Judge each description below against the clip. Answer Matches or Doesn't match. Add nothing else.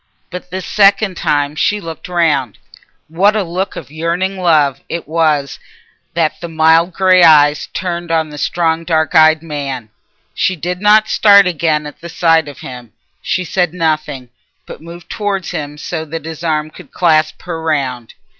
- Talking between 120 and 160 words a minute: Doesn't match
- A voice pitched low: Doesn't match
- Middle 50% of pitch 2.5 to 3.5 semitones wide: Matches